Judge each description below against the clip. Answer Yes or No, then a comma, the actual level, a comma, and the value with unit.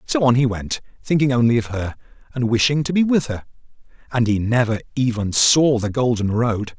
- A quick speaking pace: No, average, 195 wpm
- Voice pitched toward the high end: No, low, 120 Hz